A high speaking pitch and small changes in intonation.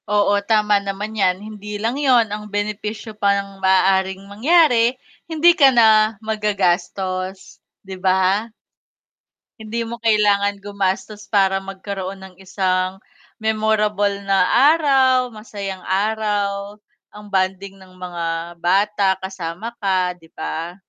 Yes: high, 200 Hz; narrow, 2.2 semitones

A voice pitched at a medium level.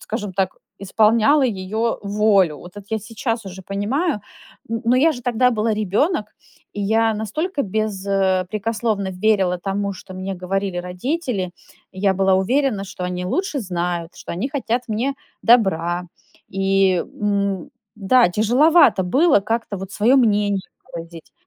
No: high, 205 Hz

